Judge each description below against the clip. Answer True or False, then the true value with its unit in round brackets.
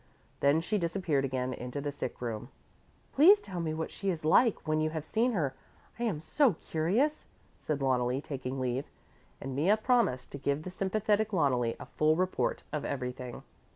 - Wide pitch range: True (6.5 semitones)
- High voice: False (155 Hz)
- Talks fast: False (180 wpm)